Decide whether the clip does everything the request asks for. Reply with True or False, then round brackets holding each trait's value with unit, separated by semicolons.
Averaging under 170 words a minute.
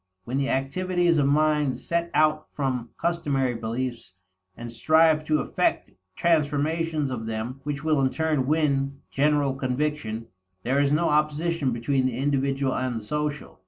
True (150 wpm)